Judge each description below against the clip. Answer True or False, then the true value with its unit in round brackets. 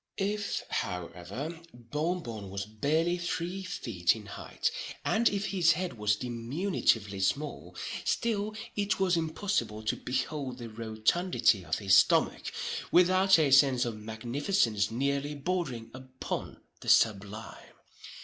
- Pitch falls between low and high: False (130 Hz)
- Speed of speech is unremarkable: False (125 wpm)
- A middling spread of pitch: False (8.2 semitones)